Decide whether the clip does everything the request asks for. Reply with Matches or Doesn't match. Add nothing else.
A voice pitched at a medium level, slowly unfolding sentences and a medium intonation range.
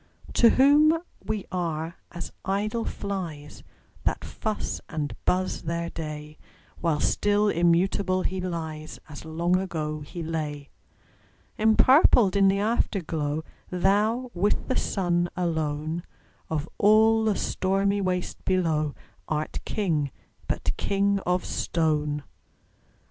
Matches